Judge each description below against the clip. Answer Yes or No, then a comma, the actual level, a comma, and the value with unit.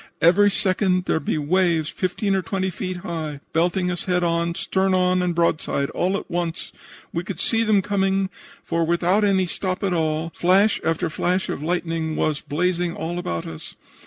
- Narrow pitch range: Yes, narrow, 2.3 semitones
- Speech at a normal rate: Yes, average, 180 wpm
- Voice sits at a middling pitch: Yes, medium, 180 Hz